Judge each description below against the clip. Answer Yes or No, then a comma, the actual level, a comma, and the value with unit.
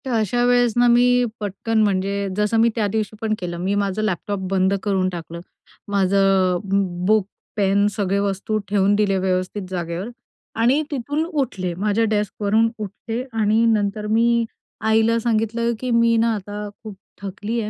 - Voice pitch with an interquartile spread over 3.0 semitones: No, average, 2.7 semitones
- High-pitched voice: Yes, high, 210 Hz